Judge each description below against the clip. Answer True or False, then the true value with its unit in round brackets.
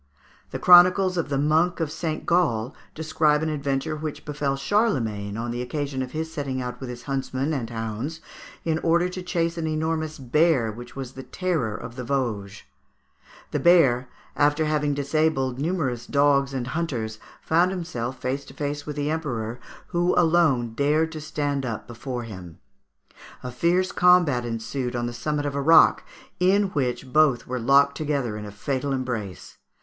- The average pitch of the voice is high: False (140 Hz)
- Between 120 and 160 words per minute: False (170 wpm)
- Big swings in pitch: False (4.4 semitones)